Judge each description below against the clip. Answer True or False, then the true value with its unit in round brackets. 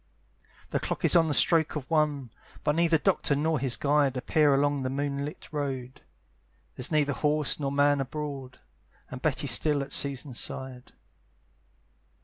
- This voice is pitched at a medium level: True (145 Hz)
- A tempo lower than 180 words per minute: True (150 wpm)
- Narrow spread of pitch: True (2.0 semitones)